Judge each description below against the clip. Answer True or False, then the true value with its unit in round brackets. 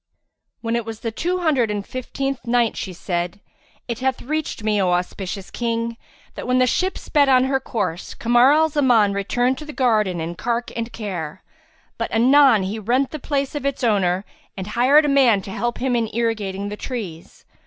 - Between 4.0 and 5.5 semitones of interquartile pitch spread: True (4.5 semitones)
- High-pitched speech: True (235 Hz)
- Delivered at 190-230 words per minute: True (195 wpm)